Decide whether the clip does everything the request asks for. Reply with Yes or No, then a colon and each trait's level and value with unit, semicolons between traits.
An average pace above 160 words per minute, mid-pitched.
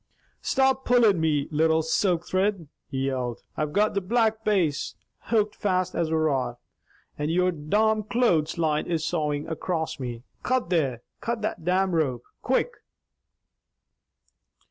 No: average, 140 wpm; medium, 170 Hz